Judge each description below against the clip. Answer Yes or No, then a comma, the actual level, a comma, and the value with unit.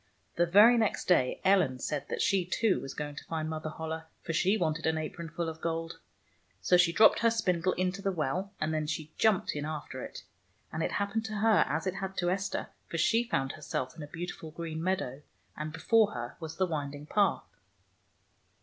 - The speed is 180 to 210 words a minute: Yes, fast, 205 wpm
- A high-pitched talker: No, medium, 165 Hz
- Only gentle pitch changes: No, average, 3.8 semitones